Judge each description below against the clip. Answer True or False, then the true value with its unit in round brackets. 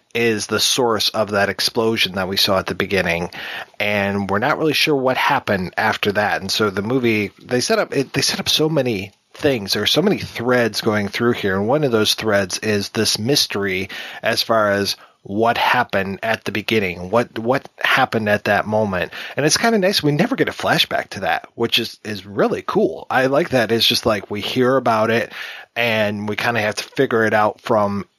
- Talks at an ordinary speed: False (215 wpm)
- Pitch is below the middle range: True (110 Hz)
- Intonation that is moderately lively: True (3.8 semitones)